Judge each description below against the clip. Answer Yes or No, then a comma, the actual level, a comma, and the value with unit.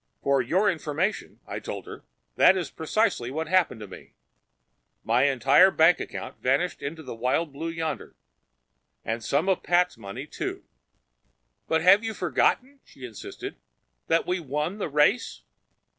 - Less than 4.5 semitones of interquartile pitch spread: No, average, 5.1 semitones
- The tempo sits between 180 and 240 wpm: No, average, 150 wpm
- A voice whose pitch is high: No, medium, 160 Hz